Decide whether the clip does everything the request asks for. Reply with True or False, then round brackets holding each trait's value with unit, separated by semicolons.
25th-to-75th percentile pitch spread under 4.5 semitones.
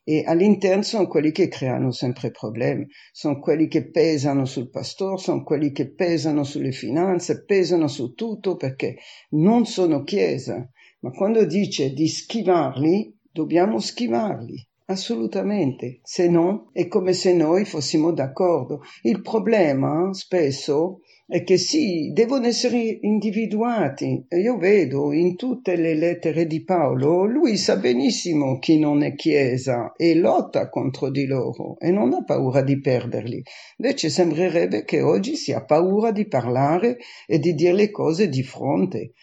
False (5.1 semitones)